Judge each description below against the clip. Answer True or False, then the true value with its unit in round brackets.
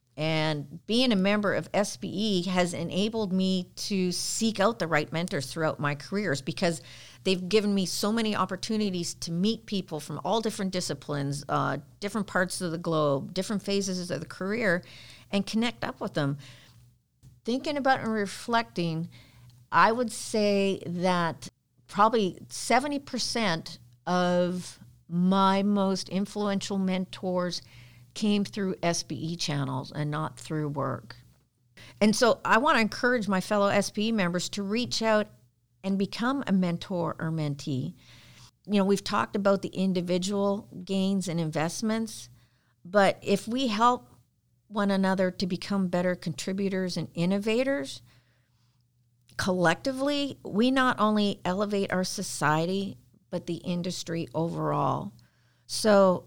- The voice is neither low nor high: True (180 Hz)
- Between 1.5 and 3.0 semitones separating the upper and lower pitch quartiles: False (5.4 semitones)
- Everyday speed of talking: False (130 wpm)